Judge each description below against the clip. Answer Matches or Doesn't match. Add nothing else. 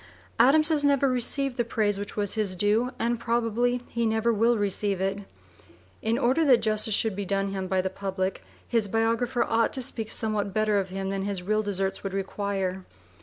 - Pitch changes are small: Doesn't match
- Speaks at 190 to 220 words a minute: Matches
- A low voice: Doesn't match